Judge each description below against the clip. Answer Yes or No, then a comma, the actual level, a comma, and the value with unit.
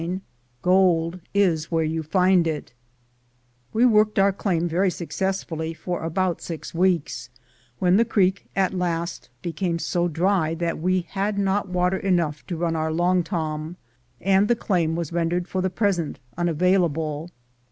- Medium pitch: Yes, medium, 175 Hz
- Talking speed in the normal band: Yes, average, 155 wpm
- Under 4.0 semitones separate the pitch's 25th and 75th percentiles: Yes, narrow, 2.6 semitones